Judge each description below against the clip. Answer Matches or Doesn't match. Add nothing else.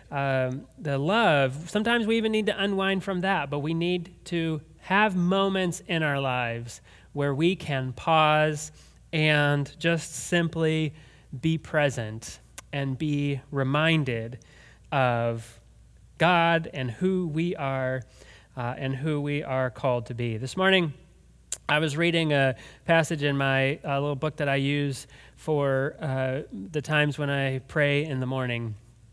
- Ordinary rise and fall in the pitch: Matches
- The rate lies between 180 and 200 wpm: Doesn't match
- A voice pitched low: Doesn't match